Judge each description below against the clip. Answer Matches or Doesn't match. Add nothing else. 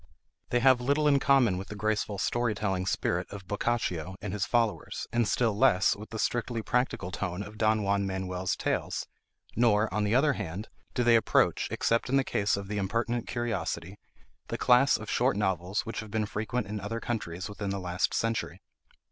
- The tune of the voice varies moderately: Matches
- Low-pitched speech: Matches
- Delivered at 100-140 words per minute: Doesn't match